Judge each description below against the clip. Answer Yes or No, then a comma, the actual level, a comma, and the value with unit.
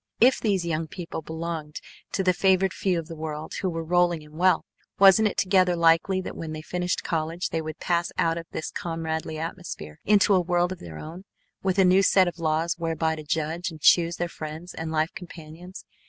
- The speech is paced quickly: Yes, fast, 210 wpm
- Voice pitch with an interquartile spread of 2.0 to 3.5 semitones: Yes, narrow, 2.4 semitones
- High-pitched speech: No, medium, 170 Hz